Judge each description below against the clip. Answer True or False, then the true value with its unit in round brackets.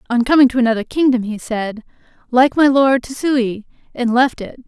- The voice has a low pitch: False (250 Hz)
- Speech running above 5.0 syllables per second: False (4.9 syllables/s)